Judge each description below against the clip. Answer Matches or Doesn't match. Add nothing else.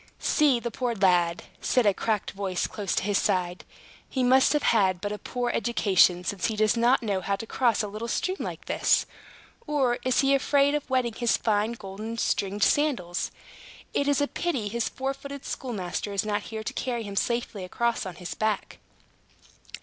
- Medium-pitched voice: Doesn't match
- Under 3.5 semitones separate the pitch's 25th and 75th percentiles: Doesn't match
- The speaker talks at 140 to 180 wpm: Doesn't match